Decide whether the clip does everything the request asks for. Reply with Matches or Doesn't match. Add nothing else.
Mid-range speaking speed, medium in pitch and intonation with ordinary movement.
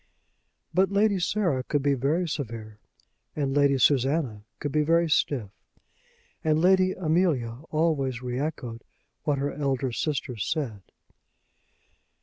Doesn't match